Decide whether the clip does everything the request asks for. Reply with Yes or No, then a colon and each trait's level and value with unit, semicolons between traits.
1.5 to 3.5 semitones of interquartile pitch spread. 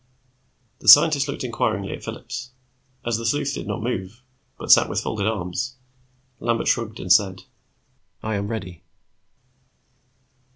No: average, 4.0 semitones